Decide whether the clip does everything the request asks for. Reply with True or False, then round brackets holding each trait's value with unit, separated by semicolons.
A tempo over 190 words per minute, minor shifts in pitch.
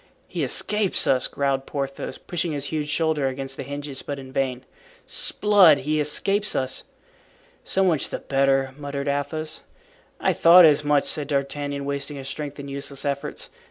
False (160 wpm; 2.0 semitones)